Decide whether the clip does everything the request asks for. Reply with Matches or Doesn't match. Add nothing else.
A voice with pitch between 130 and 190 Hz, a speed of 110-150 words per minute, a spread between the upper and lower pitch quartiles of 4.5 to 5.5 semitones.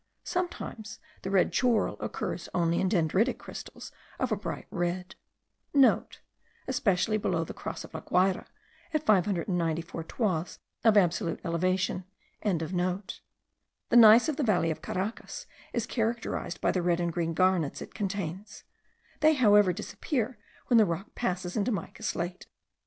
Doesn't match